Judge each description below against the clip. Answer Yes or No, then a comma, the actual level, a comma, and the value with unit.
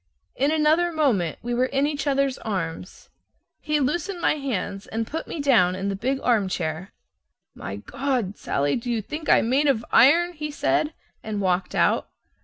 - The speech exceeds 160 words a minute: Yes, average, 175 wpm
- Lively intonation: Yes, wide, 7.2 semitones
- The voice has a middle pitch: No, very high, 255 Hz